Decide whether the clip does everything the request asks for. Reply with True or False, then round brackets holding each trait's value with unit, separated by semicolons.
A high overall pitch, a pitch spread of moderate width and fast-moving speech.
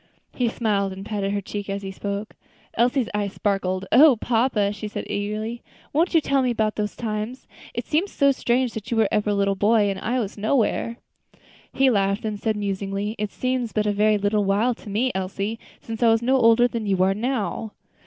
True (215 Hz; 3.0 semitones; 210 wpm)